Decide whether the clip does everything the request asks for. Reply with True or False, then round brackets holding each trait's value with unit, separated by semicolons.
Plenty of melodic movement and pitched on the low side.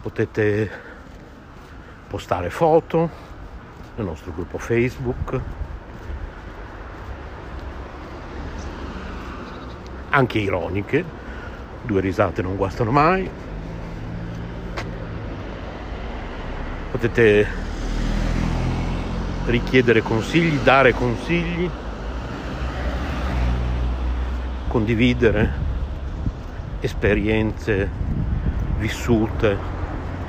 True (7.7 semitones; 90 Hz)